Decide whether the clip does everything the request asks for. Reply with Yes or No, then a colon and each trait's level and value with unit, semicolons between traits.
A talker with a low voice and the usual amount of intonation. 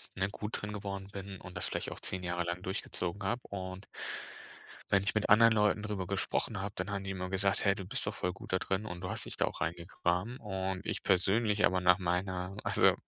No: very low, 95 Hz; narrow, 1.8 semitones